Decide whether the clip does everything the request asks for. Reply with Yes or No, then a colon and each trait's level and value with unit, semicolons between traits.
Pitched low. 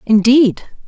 No: high, 235 Hz